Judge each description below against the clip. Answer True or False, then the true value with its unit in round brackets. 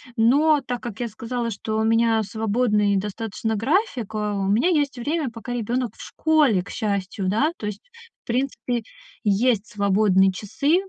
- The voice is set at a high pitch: True (225 Hz)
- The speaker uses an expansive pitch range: False (3.4 semitones)